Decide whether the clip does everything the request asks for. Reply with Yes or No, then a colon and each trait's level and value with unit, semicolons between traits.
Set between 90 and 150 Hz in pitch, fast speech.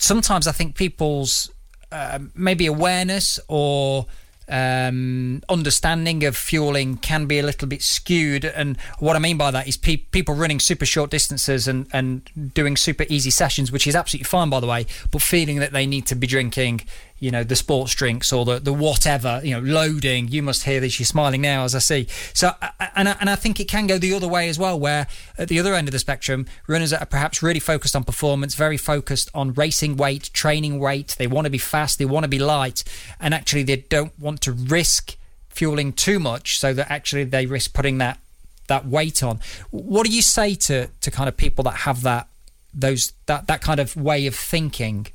Yes: medium, 140 Hz; fast, 215 wpm